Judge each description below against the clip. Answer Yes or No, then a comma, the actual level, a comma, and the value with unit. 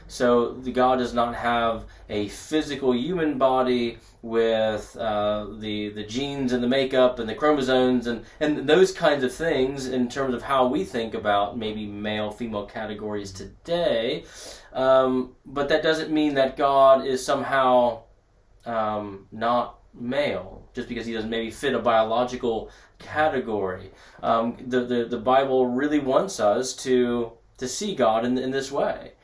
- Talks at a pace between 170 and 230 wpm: No, average, 155 wpm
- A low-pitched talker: Yes, low, 120 Hz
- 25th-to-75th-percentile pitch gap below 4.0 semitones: Yes, average, 3.0 semitones